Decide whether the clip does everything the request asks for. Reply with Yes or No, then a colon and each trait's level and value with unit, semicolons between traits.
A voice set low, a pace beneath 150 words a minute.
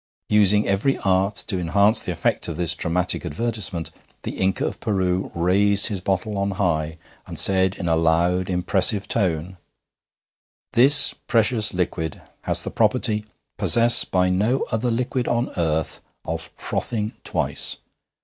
Yes: very low, 95 Hz; average, 140 wpm